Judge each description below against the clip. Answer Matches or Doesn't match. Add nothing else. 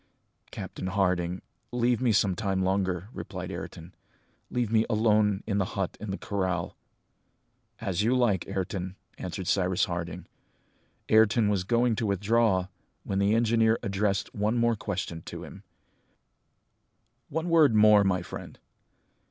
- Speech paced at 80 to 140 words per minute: Matches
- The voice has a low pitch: Matches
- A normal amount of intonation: Matches